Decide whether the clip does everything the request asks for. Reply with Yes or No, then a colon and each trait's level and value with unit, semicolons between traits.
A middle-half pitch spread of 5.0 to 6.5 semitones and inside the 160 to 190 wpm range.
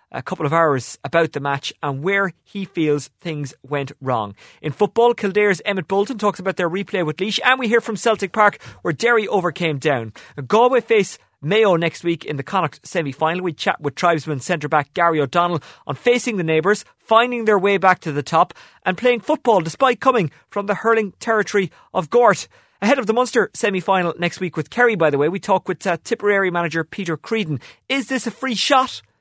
No: wide, 5.6 semitones; average, 200 wpm